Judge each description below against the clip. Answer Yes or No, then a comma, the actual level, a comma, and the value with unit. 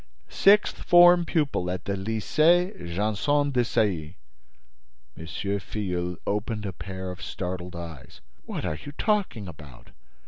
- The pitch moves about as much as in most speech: No, wide, 8.3 semitones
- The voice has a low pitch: Yes, low, 100 Hz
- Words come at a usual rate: No, slow, 130 wpm